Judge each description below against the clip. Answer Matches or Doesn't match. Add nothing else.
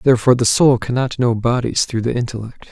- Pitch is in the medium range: Doesn't match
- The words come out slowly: Doesn't match